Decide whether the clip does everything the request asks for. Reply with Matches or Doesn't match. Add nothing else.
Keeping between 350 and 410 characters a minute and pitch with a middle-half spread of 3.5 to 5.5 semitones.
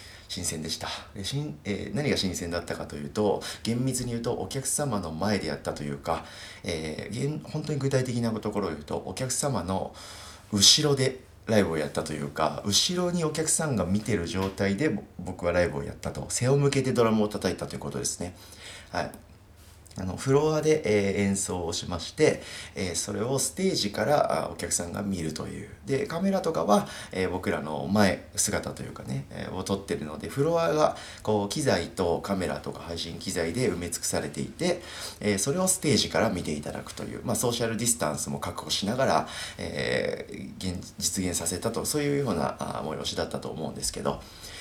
Matches